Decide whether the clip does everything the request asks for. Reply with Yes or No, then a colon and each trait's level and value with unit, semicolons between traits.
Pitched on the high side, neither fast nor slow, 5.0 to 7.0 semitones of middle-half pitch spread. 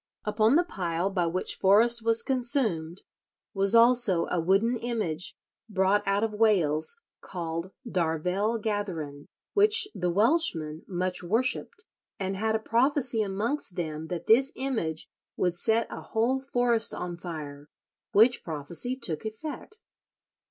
No: high, 205 Hz; slow, 130 wpm; wide, 5.4 semitones